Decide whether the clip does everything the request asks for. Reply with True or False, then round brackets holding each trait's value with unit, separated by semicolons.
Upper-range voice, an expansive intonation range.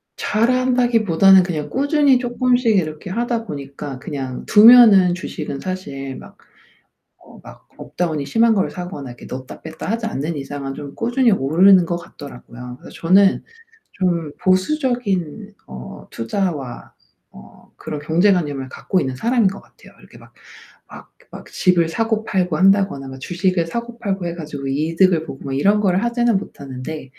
False (180 Hz; 7.0 semitones)